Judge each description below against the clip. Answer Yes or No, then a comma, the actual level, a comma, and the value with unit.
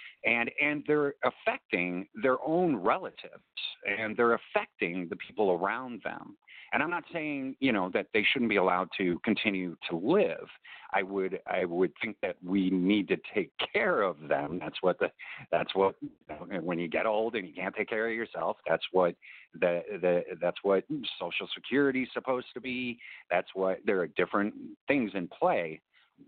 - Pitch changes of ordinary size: No, wide, 6.7 semitones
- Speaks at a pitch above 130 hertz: No, low, 110 Hz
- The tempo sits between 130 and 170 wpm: No, average, 180 wpm